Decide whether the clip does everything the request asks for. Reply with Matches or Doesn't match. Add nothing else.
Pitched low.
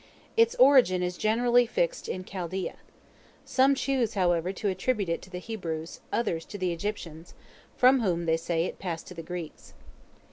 Doesn't match